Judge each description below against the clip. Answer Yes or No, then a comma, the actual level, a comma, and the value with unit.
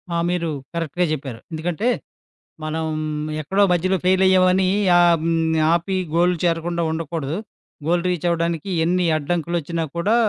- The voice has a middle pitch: Yes, medium, 170 Hz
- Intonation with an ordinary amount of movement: No, narrow, 1.8 semitones